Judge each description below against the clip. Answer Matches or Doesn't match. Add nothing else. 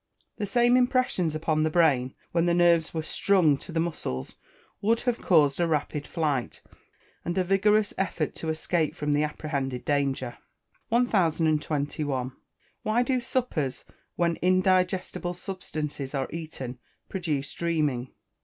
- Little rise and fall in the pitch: Doesn't match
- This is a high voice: Doesn't match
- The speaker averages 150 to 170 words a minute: Doesn't match